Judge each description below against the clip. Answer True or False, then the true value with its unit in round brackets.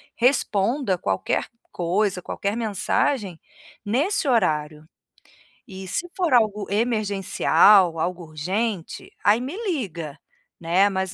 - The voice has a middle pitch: False (200 Hz)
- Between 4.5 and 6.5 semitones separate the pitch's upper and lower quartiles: True (4.8 semitones)